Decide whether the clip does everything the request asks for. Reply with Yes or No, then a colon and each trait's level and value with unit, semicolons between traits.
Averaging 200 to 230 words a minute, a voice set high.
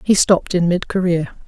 No: fast, 205 wpm; medium, 180 Hz